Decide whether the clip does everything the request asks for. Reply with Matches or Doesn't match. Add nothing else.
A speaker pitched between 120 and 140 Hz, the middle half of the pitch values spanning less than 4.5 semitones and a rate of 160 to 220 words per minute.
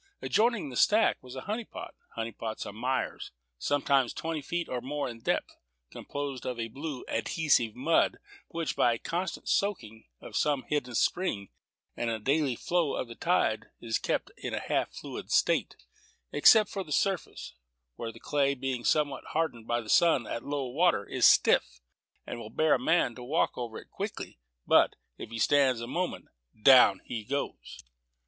Doesn't match